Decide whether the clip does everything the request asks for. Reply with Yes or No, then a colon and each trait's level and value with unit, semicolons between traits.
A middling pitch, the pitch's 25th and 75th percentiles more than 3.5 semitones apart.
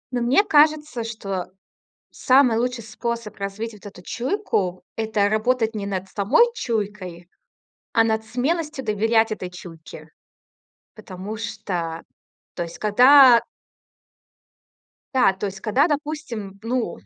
No: high, 220 Hz; average, 4.1 semitones